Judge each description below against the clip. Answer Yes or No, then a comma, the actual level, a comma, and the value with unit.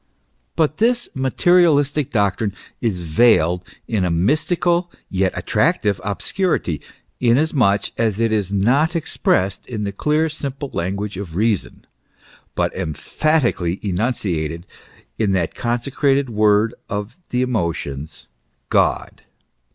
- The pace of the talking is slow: Yes, slow, 110 wpm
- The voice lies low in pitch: Yes, low, 110 Hz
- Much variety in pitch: Yes, wide, 6.8 semitones